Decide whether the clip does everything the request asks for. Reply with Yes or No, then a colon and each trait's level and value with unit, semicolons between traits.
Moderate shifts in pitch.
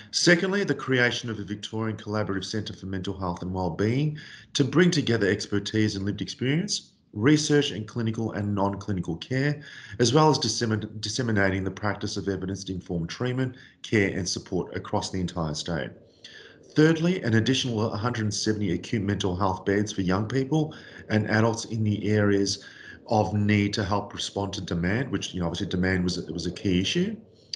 Yes: average, 4.1 semitones